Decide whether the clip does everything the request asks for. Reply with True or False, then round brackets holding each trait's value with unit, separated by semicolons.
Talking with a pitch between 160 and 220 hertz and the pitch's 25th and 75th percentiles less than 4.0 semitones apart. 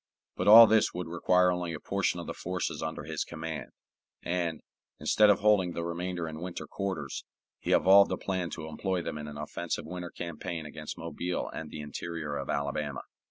False (85 Hz; 2.7 semitones)